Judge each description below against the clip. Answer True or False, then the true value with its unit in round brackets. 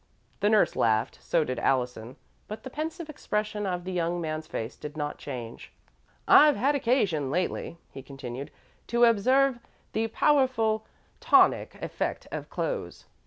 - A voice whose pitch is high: True (200 Hz)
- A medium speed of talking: True (145 wpm)